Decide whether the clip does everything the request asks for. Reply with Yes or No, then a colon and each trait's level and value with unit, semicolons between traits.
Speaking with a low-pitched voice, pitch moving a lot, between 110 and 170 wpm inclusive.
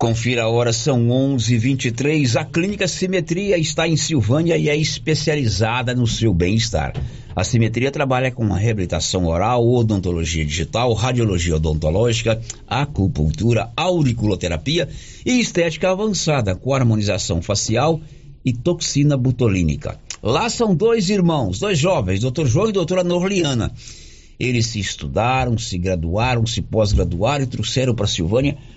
Yes: low, 120 Hz; wide, 5.8 semitones; average, 130 wpm